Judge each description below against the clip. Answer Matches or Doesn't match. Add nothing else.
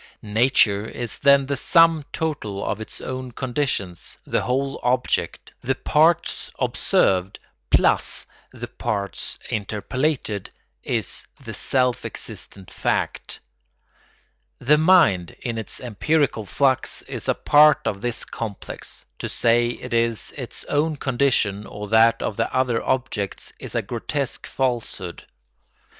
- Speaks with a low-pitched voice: Matches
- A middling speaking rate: Doesn't match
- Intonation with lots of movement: Doesn't match